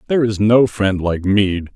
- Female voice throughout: No, male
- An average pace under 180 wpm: No, fast, 205 wpm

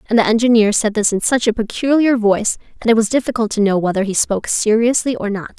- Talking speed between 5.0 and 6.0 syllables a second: No, 6.3 syllables/s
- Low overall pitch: No, high, 220 Hz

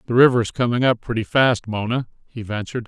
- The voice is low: Yes, low, 115 Hz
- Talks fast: No, average, 190 wpm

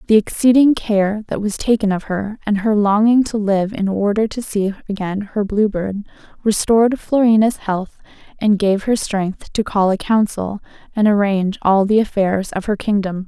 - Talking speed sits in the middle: Yes, average, 180 wpm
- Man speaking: No, female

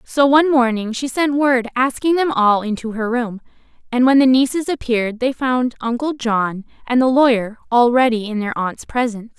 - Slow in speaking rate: No, average, 185 wpm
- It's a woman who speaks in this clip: Yes, female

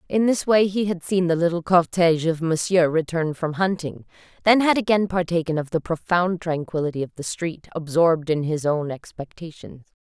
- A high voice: No, medium, 170 Hz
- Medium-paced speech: Yes, average, 180 wpm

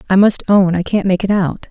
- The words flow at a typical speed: No, fast, 280 wpm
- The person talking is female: Yes, female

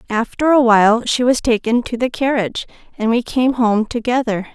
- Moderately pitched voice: No, high, 240 Hz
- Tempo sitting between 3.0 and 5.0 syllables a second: No, 5.3 syllables/s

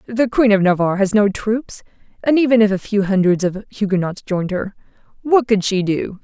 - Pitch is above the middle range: Yes, high, 205 Hz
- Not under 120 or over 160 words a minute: No, average, 200 wpm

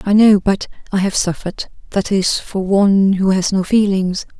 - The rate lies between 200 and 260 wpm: No, average, 190 wpm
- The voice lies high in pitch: Yes, high, 195 Hz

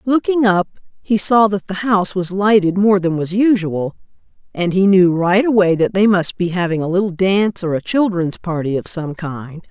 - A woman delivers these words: Yes, female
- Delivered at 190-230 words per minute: Yes, fast, 205 wpm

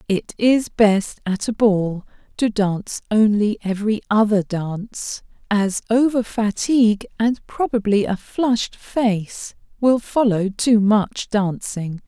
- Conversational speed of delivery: No, slow, 125 wpm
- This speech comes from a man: No, female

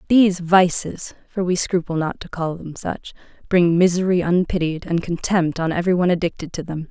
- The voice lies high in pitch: No, medium, 175 Hz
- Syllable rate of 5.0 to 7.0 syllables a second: No, 4.6 syllables/s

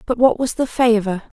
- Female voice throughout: Yes, female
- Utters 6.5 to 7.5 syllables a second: No, 5.0 syllables/s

